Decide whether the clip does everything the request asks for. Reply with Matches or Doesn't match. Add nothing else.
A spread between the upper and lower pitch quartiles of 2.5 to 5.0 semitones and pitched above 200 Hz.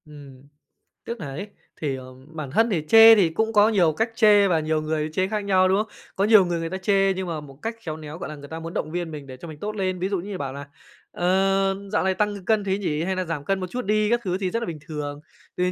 Doesn't match